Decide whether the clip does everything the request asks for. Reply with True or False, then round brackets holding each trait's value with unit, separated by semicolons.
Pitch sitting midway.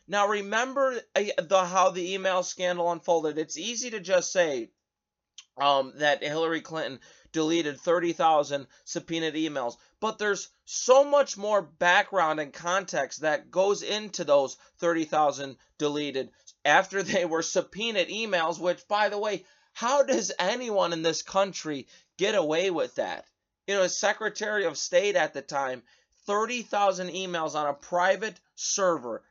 True (180 Hz)